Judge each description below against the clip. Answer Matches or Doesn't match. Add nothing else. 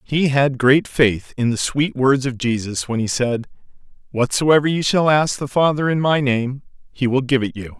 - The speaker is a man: Matches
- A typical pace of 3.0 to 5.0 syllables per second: Matches